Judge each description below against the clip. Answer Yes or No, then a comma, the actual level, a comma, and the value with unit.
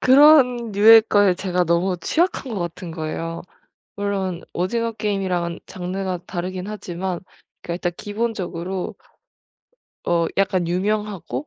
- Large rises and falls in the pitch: No, average, 3.2 semitones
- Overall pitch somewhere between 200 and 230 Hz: No, high, 190 Hz